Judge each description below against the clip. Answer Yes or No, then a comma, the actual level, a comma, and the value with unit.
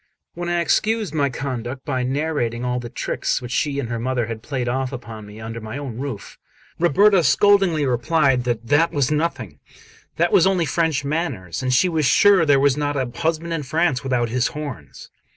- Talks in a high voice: No, medium, 140 Hz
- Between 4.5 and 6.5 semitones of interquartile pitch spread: Yes, average, 4.8 semitones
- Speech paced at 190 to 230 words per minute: Yes, average, 195 wpm